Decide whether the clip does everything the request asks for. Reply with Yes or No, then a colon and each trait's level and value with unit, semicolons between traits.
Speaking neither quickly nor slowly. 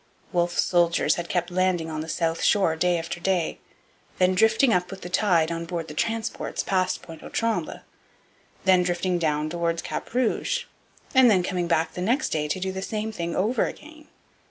Yes: average, 190 wpm